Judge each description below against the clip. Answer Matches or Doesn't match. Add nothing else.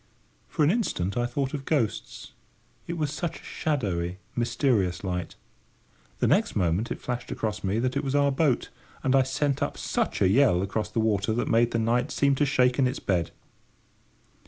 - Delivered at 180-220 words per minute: Matches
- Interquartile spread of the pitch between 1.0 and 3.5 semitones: Doesn't match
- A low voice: Matches